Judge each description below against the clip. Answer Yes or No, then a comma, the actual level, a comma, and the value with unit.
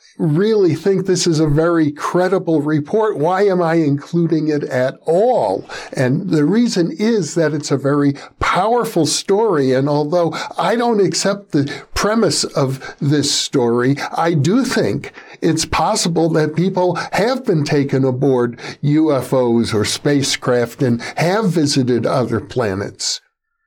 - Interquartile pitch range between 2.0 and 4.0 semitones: No, average, 4.7 semitones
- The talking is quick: No, slow, 135 wpm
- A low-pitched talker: No, medium, 160 Hz